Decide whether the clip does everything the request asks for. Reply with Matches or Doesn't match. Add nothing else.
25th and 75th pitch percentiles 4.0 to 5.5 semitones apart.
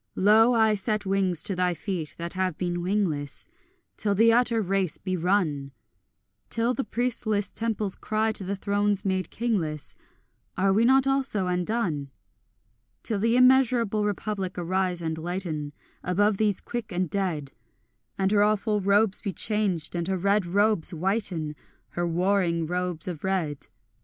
Doesn't match